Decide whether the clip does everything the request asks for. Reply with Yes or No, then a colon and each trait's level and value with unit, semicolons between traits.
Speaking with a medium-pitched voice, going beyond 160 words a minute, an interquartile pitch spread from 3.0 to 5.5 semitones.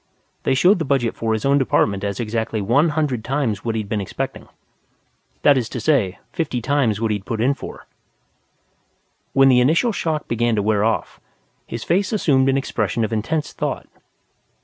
No: low, 120 Hz; average, 180 wpm; average, 4.5 semitones